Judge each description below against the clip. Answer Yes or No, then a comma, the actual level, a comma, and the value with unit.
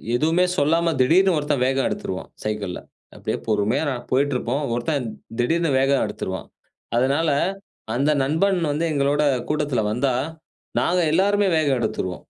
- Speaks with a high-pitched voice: No, medium, 145 Hz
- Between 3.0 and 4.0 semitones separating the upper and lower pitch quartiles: No, average, 4.6 semitones